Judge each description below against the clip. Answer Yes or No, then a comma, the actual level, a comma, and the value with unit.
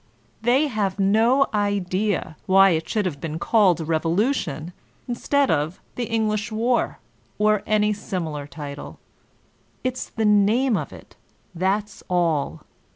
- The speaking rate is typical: No, slow, 130 wpm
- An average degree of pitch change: Yes, average, 4.5 semitones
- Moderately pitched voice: No, high, 205 Hz